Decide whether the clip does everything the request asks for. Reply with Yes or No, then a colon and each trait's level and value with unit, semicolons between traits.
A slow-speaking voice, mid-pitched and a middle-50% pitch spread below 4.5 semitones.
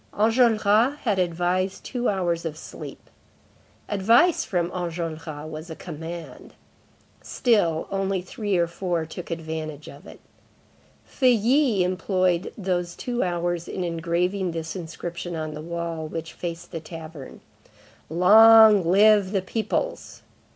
Yes: slow, 125 wpm; medium, 175 Hz; average, 3.6 semitones